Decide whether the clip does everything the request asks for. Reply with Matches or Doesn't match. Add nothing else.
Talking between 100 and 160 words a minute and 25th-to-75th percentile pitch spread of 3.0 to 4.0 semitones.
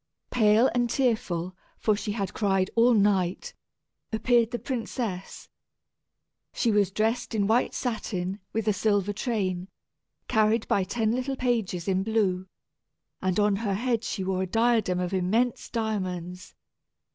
Matches